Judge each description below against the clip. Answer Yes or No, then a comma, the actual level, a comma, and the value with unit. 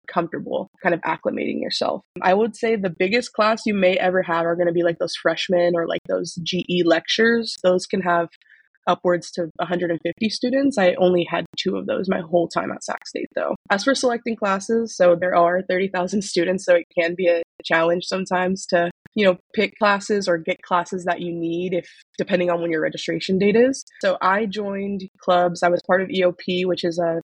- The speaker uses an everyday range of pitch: No, narrow, 2.3 semitones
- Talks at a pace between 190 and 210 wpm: Yes, fast, 205 wpm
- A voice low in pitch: No, medium, 180 Hz